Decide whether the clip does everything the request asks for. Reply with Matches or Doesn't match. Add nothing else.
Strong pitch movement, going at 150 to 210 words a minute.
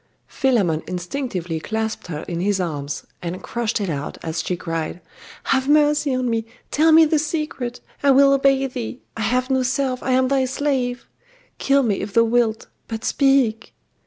Matches